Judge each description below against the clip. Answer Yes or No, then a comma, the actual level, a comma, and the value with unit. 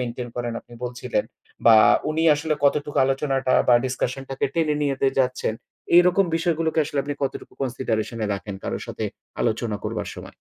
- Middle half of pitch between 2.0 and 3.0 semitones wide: No, average, 3.8 semitones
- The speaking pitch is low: Yes, low, 130 Hz